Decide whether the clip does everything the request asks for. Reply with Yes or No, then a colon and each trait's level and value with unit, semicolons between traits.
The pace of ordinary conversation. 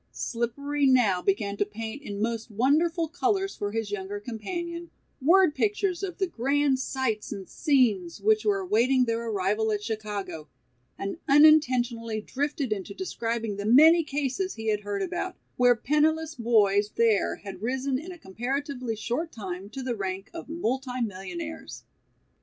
Yes: average, 150 wpm